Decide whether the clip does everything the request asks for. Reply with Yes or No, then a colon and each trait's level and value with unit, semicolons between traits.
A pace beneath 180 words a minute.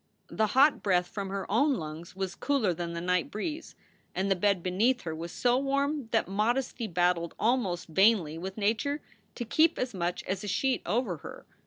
No: average, 190 wpm